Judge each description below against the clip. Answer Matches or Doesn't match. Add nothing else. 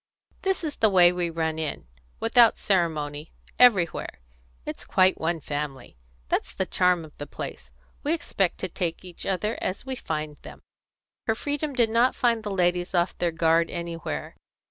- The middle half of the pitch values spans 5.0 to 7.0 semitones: Matches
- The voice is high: Doesn't match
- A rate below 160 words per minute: Doesn't match